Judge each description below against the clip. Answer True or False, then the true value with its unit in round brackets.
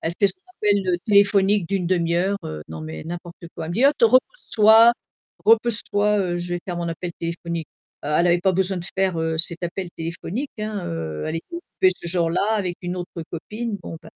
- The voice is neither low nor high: True (180 Hz)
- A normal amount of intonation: True (3.3 semitones)